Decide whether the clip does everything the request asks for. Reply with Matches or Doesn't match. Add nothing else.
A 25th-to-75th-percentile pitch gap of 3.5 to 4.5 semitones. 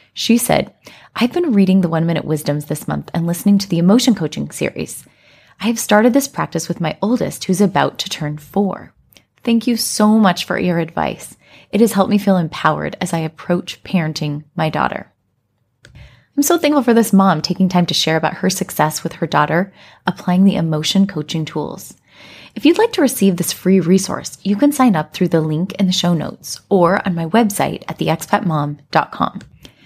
Matches